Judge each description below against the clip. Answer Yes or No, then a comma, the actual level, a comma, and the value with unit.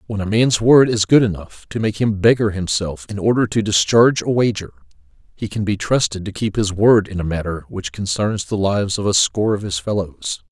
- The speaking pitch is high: No, low, 105 Hz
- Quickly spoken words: Yes, fast, 225 wpm